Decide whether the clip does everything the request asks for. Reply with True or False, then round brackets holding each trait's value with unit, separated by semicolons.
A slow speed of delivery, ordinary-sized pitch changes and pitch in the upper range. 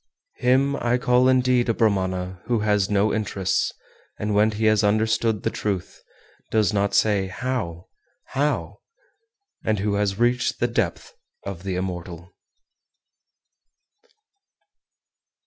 False (125 wpm; 3.7 semitones; 105 Hz)